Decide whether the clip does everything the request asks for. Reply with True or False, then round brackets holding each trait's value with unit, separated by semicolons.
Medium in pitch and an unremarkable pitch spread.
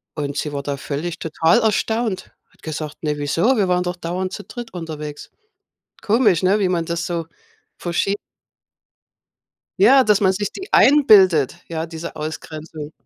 True (175 Hz; 4.6 semitones)